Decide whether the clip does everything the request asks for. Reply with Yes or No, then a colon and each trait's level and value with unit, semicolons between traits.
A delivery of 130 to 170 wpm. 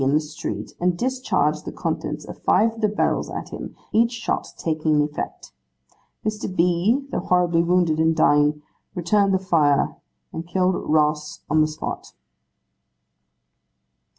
Yes: average, 145 wpm